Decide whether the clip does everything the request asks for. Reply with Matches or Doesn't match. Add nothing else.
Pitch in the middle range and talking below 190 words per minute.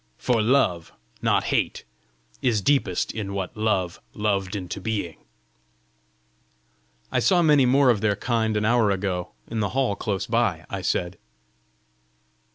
Doesn't match